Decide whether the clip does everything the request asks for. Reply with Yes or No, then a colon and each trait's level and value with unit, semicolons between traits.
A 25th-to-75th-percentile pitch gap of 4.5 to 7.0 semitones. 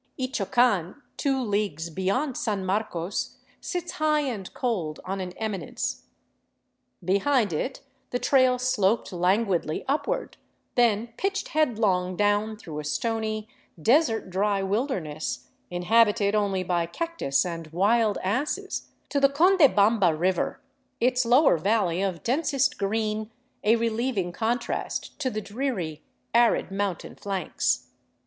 Yes: average, 5.3 semitones